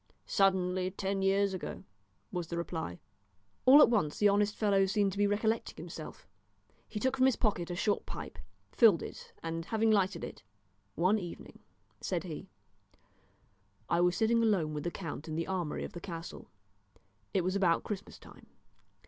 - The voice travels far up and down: No, average, 3.2 semitones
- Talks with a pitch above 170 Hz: Yes, high, 190 Hz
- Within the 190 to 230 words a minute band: No, average, 170 wpm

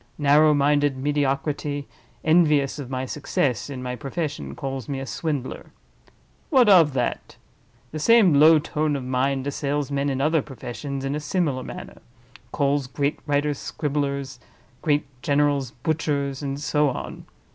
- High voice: No, medium, 145 Hz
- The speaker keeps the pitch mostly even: Yes, narrow, 1.7 semitones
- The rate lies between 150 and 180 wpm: No, slow, 135 wpm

